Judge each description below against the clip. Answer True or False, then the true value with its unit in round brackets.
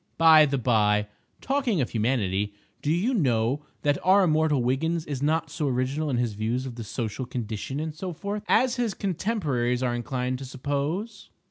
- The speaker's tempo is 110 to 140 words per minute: False (175 wpm)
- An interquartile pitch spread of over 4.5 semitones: True (5.1 semitones)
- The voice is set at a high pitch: False (140 Hz)